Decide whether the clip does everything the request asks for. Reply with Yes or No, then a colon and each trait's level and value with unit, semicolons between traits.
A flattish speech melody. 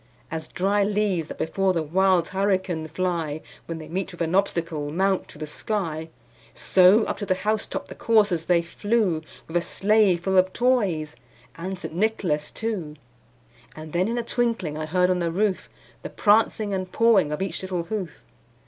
No: average, 3.8 semitones